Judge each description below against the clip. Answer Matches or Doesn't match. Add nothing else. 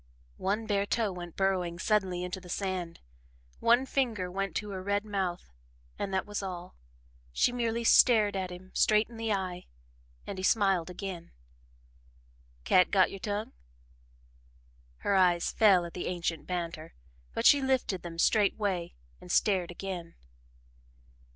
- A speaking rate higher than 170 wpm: Doesn't match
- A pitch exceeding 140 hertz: Matches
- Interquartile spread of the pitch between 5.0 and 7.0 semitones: Doesn't match